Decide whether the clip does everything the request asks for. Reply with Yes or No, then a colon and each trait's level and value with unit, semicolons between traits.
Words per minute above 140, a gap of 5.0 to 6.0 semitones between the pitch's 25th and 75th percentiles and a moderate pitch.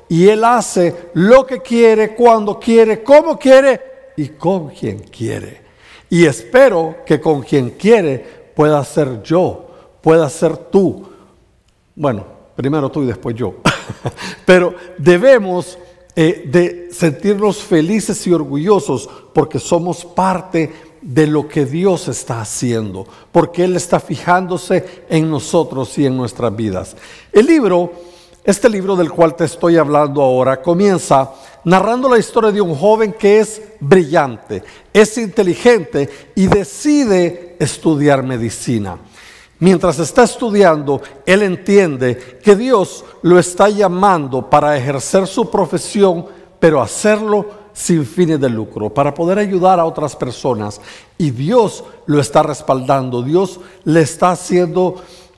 No: average, 130 wpm; average, 5.3 semitones; medium, 175 Hz